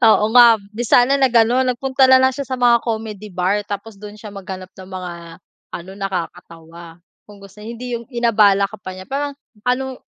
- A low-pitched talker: No, high, 220 Hz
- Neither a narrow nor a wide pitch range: Yes, average, 4.1 semitones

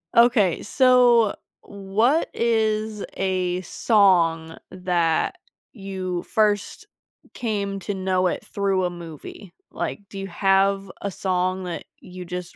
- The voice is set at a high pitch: Yes, high, 195 Hz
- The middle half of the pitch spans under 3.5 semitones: Yes, narrow, 2.6 semitones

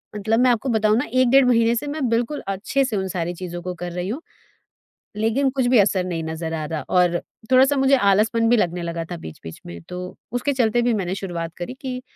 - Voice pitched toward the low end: No, high, 215 Hz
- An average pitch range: No, wide, 6.1 semitones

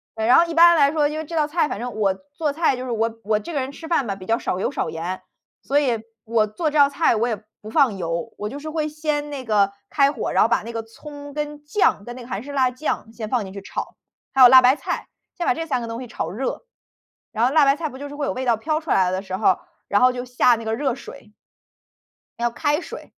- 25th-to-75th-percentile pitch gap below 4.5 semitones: No, average, 5.0 semitones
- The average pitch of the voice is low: No, very high, 255 Hz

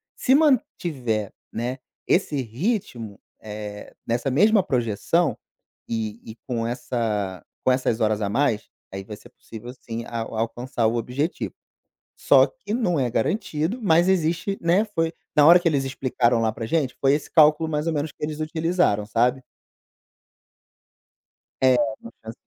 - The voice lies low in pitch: Yes, low, 130 Hz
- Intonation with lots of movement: Yes, wide, 6.3 semitones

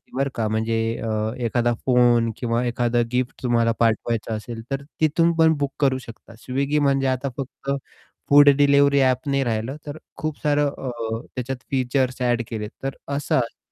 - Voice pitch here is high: No, low, 130 Hz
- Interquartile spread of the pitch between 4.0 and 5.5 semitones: No, average, 3.0 semitones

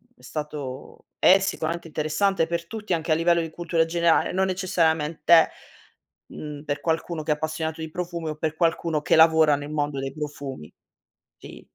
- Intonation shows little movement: Yes, narrow, 2.1 semitones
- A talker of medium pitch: Yes, medium, 160 Hz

